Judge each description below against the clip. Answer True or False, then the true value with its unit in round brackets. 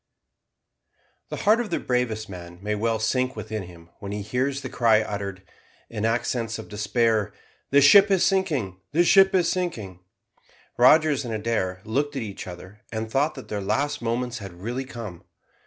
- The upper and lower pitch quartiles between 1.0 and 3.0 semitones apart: False (5.1 semitones)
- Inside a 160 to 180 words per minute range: True (170 wpm)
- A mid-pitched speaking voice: False (115 Hz)